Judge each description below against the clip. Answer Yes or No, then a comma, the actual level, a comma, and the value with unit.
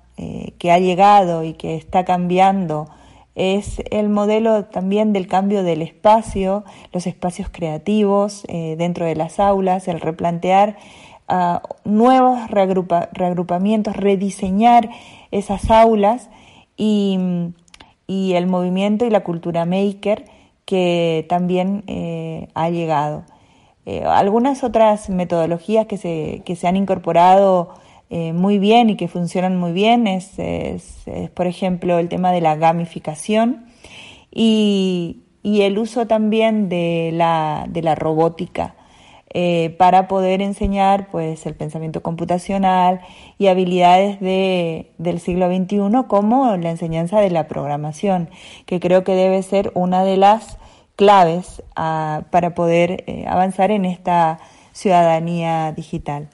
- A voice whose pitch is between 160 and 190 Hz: Yes, medium, 185 Hz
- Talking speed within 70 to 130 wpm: Yes, slow, 125 wpm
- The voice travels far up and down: No, average, 3.0 semitones